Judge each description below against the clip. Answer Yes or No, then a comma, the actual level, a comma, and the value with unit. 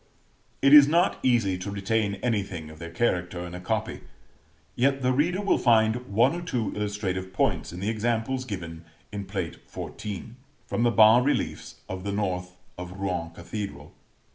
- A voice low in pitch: Yes, low, 105 Hz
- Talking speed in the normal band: Yes, average, 165 wpm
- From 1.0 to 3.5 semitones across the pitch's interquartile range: No, average, 4.7 semitones